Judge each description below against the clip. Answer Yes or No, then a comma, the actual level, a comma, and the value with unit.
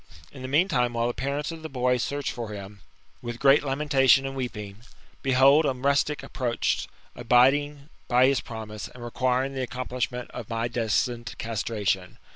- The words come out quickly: No, average, 165 wpm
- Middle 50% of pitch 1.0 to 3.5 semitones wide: Yes, average, 2.7 semitones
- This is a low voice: Yes, low, 125 Hz